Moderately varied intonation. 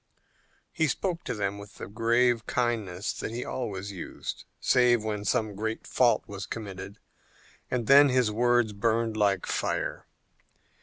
Yes: average, 3.1 semitones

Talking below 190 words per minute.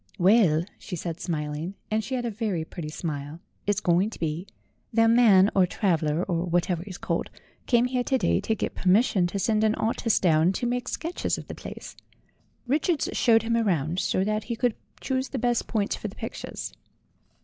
No: average, 195 wpm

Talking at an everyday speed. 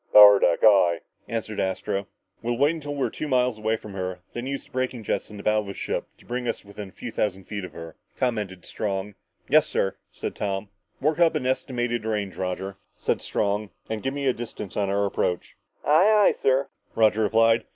No: fast, 215 wpm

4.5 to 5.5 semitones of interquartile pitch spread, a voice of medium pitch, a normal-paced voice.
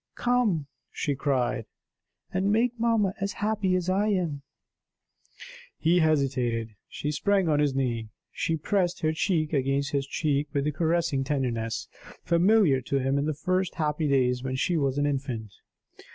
Yes: average, 5.2 semitones; medium, 150 Hz; average, 155 wpm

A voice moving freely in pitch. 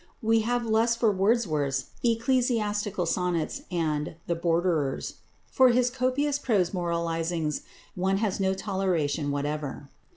Yes: wide, 5.8 semitones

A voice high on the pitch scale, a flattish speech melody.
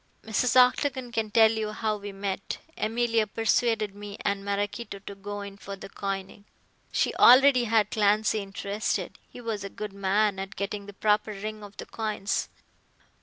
Yes: high, 210 Hz; narrow, 1.9 semitones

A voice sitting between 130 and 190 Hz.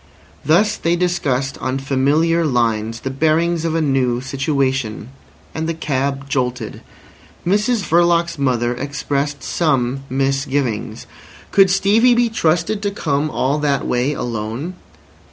Yes: medium, 140 Hz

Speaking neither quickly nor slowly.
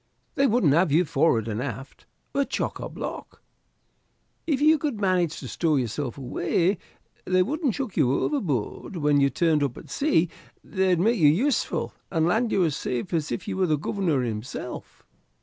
Yes: average, 180 wpm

